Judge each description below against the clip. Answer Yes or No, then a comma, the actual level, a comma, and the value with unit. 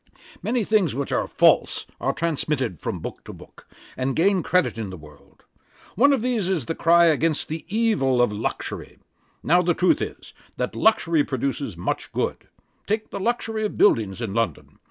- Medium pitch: Yes, medium, 165 Hz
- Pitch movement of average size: No, wide, 8.4 semitones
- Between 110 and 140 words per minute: No, average, 175 wpm